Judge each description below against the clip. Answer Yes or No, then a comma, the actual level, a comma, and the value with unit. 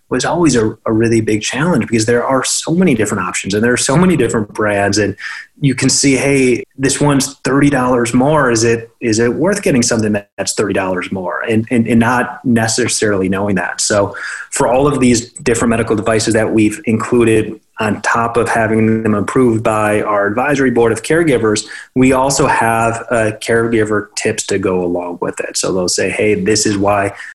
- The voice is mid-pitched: No, low, 115 Hz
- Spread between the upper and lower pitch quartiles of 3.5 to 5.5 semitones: No, average, 2.7 semitones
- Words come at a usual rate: Yes, average, 195 wpm